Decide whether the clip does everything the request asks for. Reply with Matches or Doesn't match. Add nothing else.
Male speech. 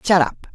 Doesn't match